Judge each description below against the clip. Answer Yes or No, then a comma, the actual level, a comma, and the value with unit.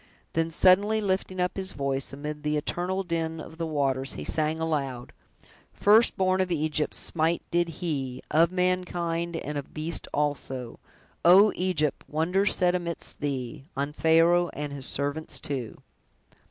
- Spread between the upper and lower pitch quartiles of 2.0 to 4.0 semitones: Yes, average, 3.7 semitones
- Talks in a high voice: No, medium, 160 Hz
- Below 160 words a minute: Yes, average, 150 wpm